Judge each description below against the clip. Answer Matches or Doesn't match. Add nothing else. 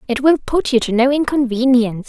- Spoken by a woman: Matches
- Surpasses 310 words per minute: Doesn't match